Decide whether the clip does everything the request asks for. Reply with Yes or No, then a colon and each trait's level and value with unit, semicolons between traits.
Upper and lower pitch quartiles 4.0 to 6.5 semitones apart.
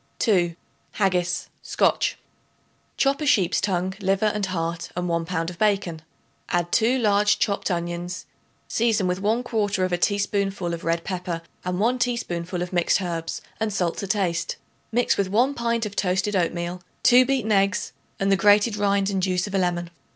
No: average, 3.1 semitones